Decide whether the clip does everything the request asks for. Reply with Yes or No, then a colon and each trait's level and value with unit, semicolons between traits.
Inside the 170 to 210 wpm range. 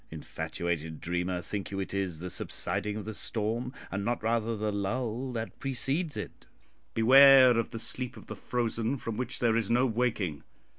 Yes: average, 180 wpm